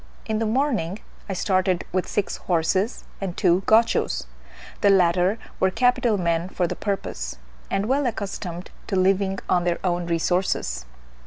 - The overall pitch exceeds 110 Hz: Yes, high, 190 Hz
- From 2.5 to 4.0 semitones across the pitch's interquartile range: Yes, average, 2.9 semitones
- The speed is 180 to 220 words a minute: No, average, 150 wpm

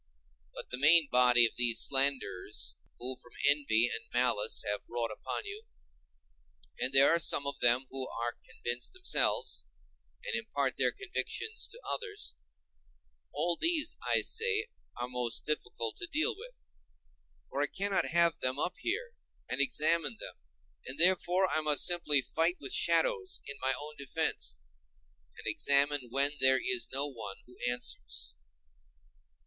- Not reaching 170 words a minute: Yes, average, 145 wpm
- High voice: No, medium, 140 Hz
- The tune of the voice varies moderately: No, wide, 7.5 semitones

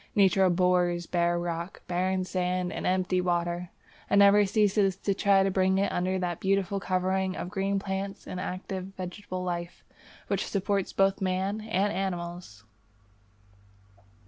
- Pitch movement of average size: No, narrow, 1.5 semitones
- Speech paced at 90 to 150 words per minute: Yes, average, 145 wpm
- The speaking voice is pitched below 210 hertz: Yes, medium, 185 Hz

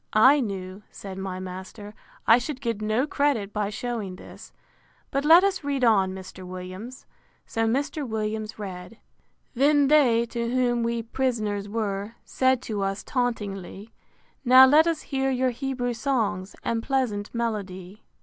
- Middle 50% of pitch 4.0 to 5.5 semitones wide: Yes, average, 4.4 semitones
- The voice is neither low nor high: No, high, 230 Hz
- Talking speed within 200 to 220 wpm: No, average, 150 wpm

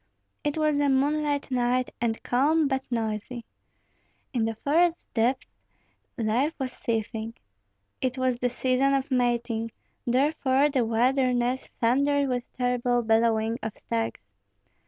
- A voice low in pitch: No, very high, 250 Hz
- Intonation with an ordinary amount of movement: Yes, average, 3.0 semitones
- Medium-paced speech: No, slow, 125 wpm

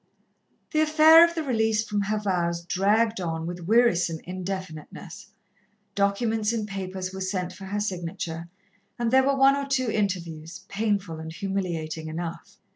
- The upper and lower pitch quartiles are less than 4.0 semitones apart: No, average, 4.4 semitones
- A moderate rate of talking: Yes, average, 150 wpm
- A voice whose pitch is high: Yes, high, 195 Hz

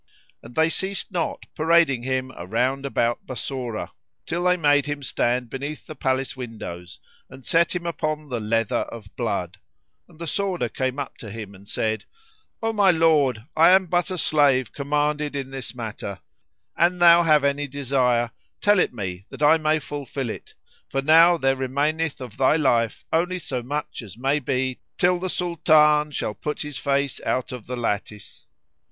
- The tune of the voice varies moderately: Yes, average, 4.6 semitones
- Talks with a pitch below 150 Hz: Yes, medium, 140 Hz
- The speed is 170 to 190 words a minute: Yes, average, 175 wpm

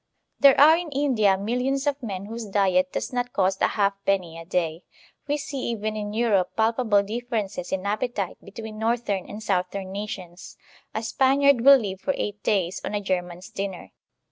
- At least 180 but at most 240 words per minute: Yes, average, 185 wpm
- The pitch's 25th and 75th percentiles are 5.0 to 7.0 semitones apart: No, average, 4.1 semitones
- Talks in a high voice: Yes, high, 210 Hz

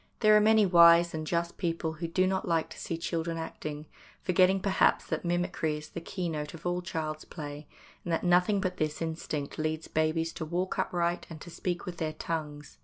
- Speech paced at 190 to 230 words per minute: Yes, average, 200 wpm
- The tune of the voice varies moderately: No, narrow, 2.3 semitones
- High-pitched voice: No, medium, 170 Hz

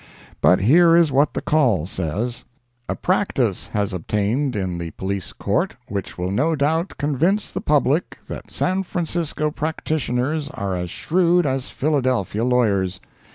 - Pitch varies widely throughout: Yes, wide, 8.0 semitones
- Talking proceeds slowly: No, average, 145 wpm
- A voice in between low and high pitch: No, low, 130 Hz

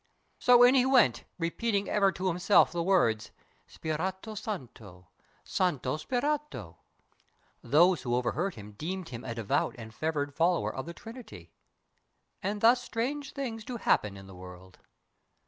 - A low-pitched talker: No, medium, 175 Hz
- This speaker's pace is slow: No, average, 145 wpm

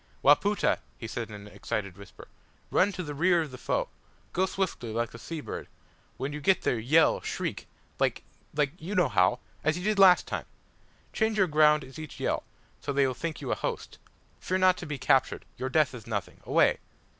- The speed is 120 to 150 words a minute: No, fast, 205 wpm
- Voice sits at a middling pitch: Yes, medium, 150 Hz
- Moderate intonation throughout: No, wide, 6.6 semitones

